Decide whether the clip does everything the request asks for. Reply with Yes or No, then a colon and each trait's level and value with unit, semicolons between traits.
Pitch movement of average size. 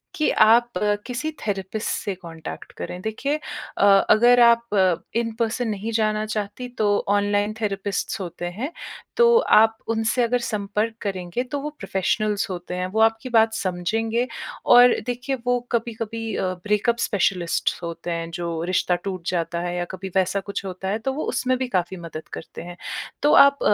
Yes: average, 4.1 semitones